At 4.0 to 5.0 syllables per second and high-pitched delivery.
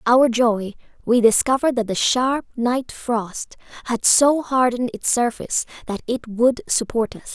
Yes: 4.6 syllables/s; high, 245 Hz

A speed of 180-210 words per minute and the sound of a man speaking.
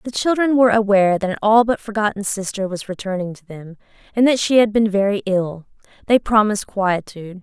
No: average, 195 wpm; female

